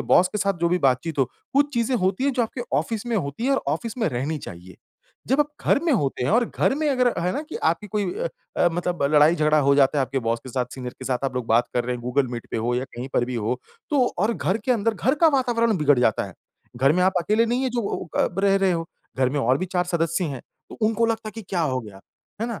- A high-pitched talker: No, medium, 175 Hz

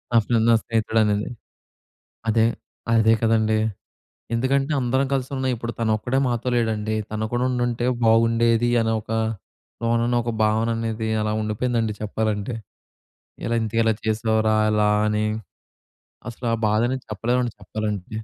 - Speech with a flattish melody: Yes, narrow, 1.7 semitones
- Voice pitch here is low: Yes, low, 115 Hz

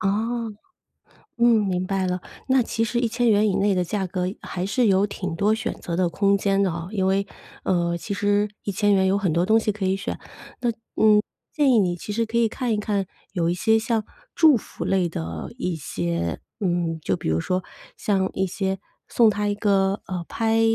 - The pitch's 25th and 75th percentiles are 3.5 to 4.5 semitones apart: No, average, 3.1 semitones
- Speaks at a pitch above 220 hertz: No, high, 200 Hz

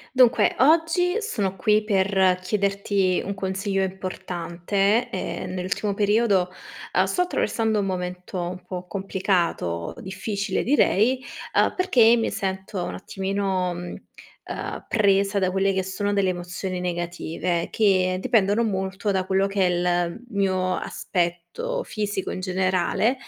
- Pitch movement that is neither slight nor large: No, narrow, 1.9 semitones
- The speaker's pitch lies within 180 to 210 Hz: Yes, high, 190 Hz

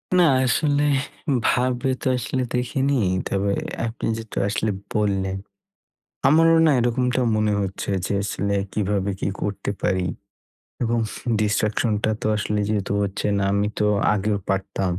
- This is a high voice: No, low, 105 Hz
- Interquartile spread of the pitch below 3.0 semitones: No, average, 3.7 semitones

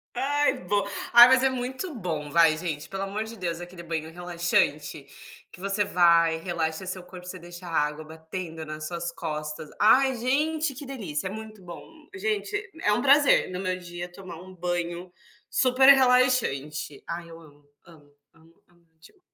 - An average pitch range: No, wide, 5.8 semitones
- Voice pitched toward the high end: No, medium, 180 Hz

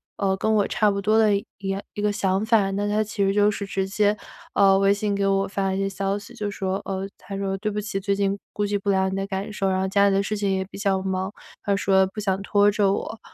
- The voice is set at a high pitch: Yes, high, 200 Hz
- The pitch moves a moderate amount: No, narrow, 1.1 semitones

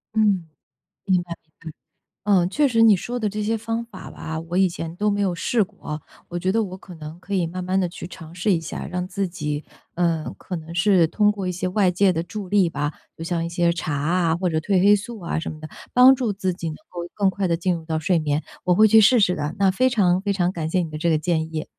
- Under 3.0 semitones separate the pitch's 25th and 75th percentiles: No, average, 3.4 semitones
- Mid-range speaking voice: Yes, medium, 180 Hz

